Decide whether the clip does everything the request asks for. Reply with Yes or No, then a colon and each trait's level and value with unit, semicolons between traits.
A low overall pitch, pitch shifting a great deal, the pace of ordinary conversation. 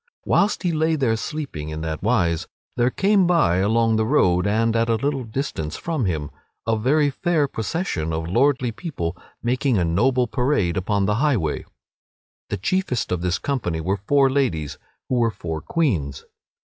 Yes: low, 115 Hz; wide, 8.0 semitones; average, 170 wpm